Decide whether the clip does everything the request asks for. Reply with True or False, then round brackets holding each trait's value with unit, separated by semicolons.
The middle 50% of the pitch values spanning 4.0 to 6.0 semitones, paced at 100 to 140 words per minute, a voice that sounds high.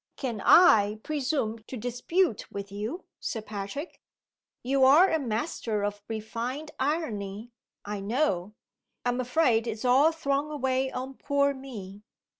True (4.8 semitones; 135 wpm; 250 Hz)